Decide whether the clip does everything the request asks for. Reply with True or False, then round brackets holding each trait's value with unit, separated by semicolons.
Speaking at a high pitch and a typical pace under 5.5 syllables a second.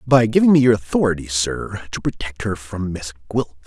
False (105 Hz; 5.3 syllables/s)